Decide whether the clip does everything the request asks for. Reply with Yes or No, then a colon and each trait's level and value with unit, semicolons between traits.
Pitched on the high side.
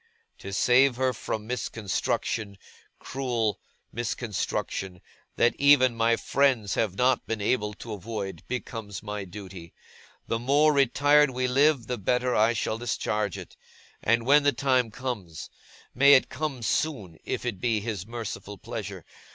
No: low, 115 Hz